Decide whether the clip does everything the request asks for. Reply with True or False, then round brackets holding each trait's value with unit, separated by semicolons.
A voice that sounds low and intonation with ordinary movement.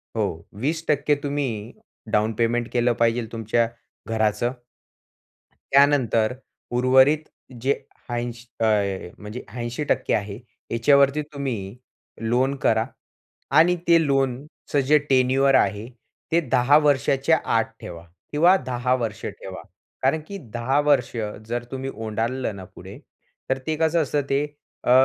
True (125 Hz; 3.7 semitones)